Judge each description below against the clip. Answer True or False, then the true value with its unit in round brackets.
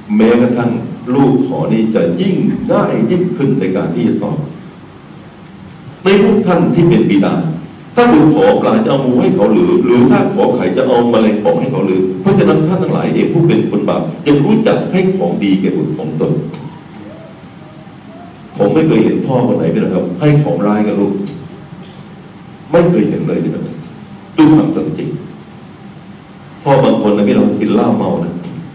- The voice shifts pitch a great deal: True (7.7 semitones)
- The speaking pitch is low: False (160 Hz)